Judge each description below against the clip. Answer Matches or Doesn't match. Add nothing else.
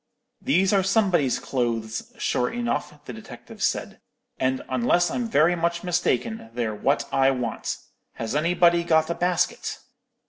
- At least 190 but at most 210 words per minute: Doesn't match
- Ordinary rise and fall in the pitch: Doesn't match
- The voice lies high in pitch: Doesn't match